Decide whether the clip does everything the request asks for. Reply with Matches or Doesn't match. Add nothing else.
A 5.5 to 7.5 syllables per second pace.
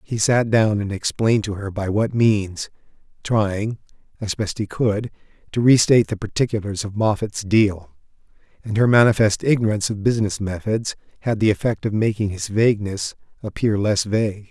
Doesn't match